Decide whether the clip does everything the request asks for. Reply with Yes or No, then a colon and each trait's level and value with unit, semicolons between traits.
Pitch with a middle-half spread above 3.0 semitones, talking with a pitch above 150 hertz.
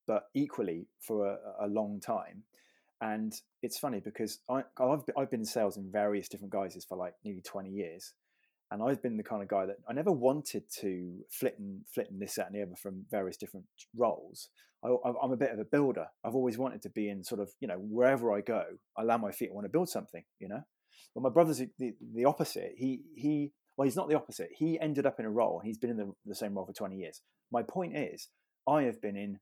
No: wide, 5.5 semitones; low, 115 Hz